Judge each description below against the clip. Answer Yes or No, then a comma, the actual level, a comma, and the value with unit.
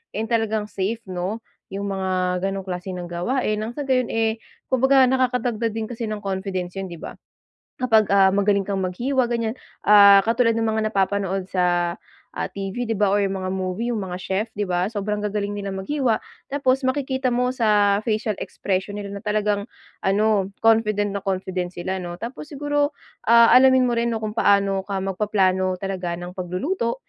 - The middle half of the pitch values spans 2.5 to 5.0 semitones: Yes, average, 3.2 semitones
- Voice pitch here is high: Yes, high, 205 Hz